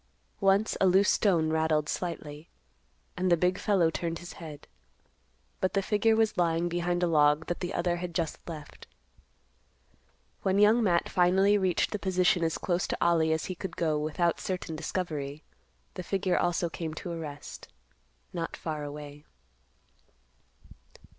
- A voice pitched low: No, medium, 175 Hz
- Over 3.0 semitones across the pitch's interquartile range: No, average, 2.7 semitones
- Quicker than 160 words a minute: No, average, 155 wpm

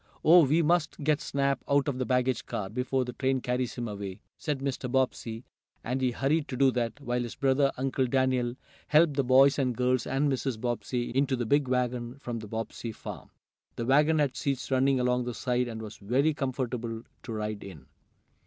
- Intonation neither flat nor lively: No, narrow, 2.3 semitones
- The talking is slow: No, average, 200 wpm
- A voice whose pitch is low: Yes, low, 130 Hz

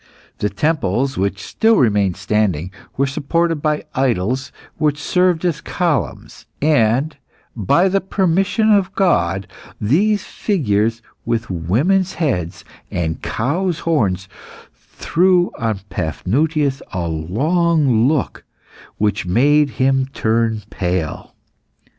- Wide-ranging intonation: Yes, wide, 8.5 semitones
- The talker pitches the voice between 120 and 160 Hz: Yes, low, 135 Hz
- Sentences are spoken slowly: Yes, slow, 105 wpm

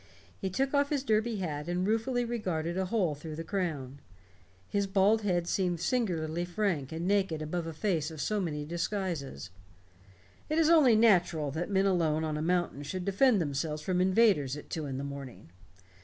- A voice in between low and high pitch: Yes, medium, 175 Hz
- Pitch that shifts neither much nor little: Yes, average, 4.9 semitones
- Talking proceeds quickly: No, average, 185 wpm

